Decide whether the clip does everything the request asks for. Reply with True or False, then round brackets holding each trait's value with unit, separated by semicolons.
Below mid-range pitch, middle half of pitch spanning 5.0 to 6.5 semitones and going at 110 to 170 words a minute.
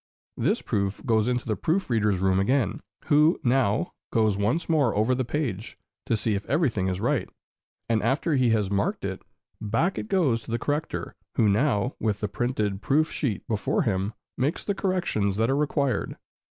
False (115 Hz; 5.5 semitones; 180 wpm)